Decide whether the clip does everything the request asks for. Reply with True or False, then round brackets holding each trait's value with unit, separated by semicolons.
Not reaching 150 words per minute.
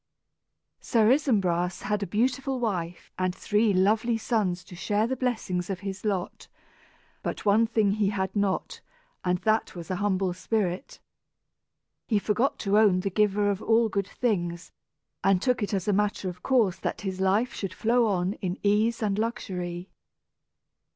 False (160 wpm)